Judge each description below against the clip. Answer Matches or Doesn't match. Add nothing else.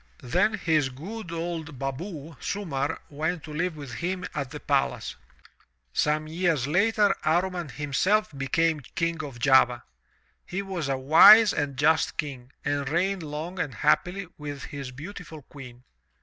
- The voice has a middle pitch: Matches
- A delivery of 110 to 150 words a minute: Matches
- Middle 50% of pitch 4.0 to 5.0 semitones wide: Matches